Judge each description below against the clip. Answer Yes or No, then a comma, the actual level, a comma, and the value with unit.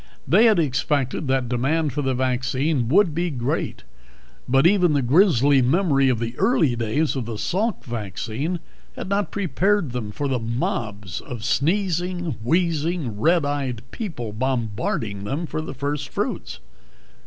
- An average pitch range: No, wide, 5.8 semitones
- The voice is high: No, medium, 140 Hz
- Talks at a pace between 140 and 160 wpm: Yes, average, 150 wpm